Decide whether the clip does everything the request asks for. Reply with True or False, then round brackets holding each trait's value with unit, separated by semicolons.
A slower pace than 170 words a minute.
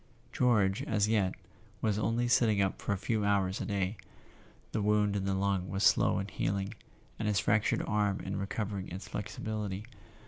False (175 wpm)